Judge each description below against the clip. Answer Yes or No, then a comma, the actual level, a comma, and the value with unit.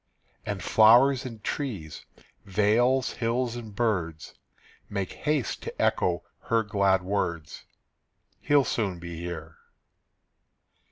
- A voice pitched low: Yes, low, 105 Hz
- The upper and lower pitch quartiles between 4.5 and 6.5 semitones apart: Yes, wide, 5.4 semitones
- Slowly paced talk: Yes, slow, 105 wpm